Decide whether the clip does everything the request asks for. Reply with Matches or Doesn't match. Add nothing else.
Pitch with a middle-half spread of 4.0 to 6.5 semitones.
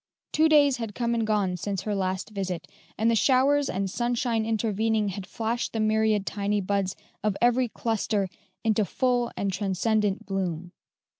Doesn't match